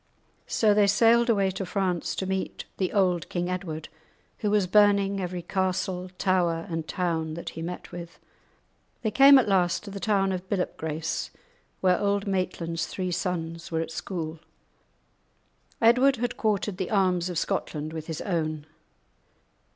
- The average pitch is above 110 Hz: Yes, medium, 185 Hz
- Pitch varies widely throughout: No, average, 3.1 semitones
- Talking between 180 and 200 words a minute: No, average, 160 wpm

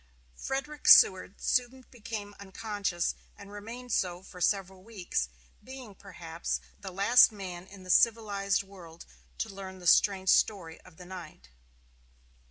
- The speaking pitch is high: Yes, high, 195 Hz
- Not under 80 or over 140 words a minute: Yes, slow, 135 wpm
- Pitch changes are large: No, average, 3.0 semitones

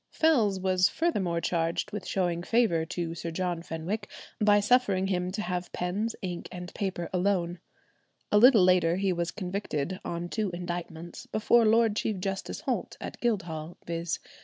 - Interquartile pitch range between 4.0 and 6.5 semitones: No, average, 3.2 semitones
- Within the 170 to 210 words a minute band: No, average, 160 wpm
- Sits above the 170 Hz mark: Yes, medium, 185 Hz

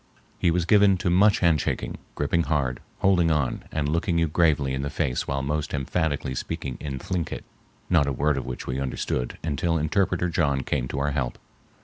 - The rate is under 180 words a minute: No, average, 190 wpm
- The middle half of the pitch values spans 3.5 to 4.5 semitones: Yes, average, 3.8 semitones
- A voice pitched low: Yes, very low, 75 Hz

